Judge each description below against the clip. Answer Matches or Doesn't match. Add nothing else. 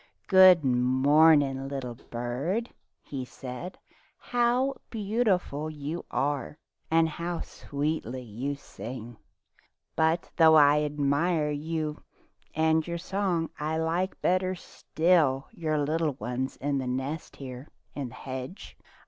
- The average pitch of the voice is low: Doesn't match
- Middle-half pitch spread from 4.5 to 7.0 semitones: Doesn't match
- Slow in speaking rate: Matches